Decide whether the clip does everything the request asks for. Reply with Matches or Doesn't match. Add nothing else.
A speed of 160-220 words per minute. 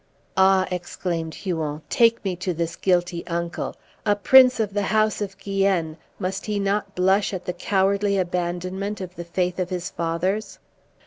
Matches